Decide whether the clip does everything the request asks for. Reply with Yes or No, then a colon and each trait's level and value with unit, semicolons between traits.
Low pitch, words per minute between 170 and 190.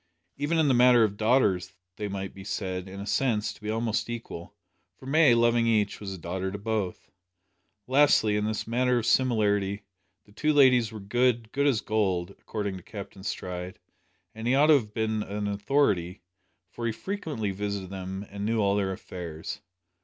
Yes: low, 105 Hz; average, 185 wpm